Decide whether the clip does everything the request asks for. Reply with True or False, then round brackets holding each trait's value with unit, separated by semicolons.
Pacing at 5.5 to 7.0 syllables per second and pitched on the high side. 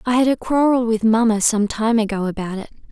True (5.8 syllables/s; 225 Hz)